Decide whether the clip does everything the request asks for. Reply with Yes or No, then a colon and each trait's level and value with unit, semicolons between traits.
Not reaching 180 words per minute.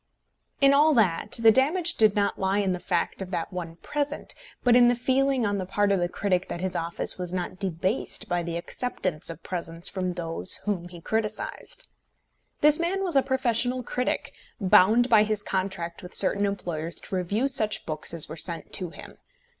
No: average, 195 wpm